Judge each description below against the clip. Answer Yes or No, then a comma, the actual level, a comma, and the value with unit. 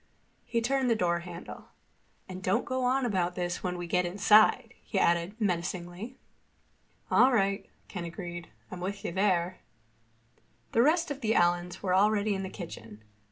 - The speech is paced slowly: No, average, 160 wpm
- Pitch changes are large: No, average, 3.7 semitones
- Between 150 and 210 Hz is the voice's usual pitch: Yes, medium, 185 Hz